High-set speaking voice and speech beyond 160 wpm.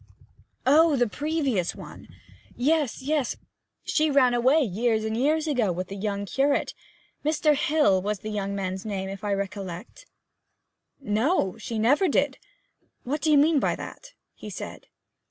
No: high, 245 Hz; average, 155 wpm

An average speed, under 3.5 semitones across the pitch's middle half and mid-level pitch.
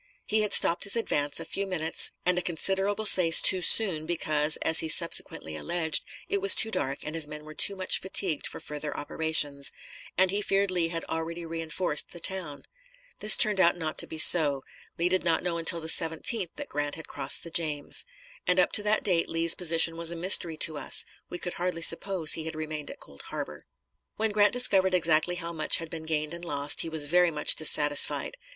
No: fast, 210 wpm; average, 3.0 semitones; medium, 165 Hz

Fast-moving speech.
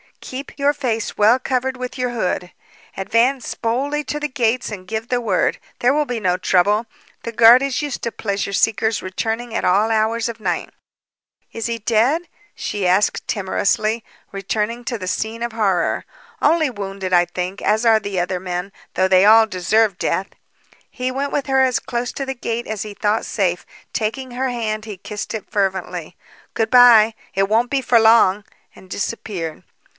No: average, 180 wpm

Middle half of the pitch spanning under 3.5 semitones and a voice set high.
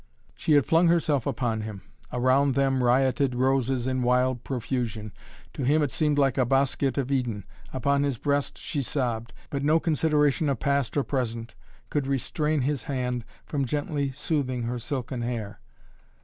No: narrow, 2.6 semitones; low, 135 Hz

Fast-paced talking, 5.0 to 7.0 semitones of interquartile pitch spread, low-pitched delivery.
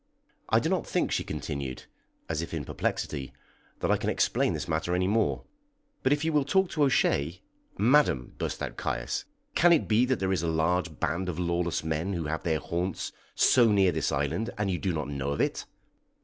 Yes: fast, 210 wpm; average, 5.3 semitones; very low, 85 Hz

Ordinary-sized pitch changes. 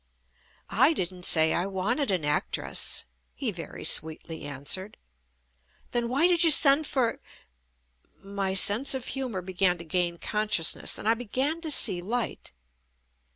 No: wide, 6.7 semitones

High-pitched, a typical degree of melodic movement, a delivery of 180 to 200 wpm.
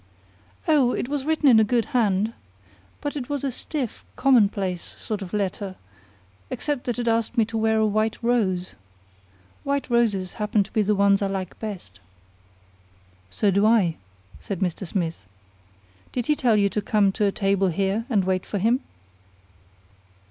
No: high, 210 Hz; average, 3.5 semitones; average, 170 wpm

